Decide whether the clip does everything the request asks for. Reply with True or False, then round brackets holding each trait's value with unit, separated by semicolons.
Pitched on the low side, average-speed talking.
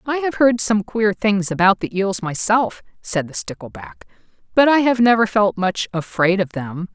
False (200 Hz; 190 wpm)